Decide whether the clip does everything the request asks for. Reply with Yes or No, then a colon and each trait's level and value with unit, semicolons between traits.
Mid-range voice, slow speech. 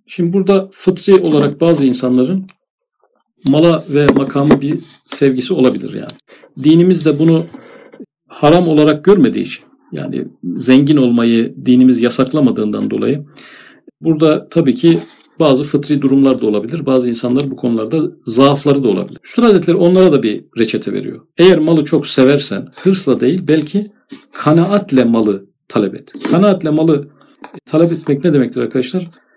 No: medium, 150 Hz; average, 135 wpm